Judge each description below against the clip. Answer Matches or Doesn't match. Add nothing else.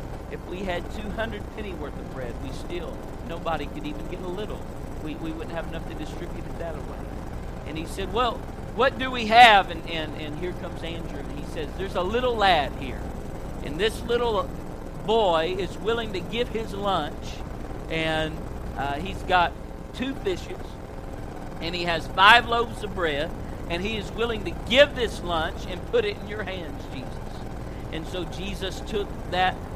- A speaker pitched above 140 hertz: Matches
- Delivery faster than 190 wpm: Doesn't match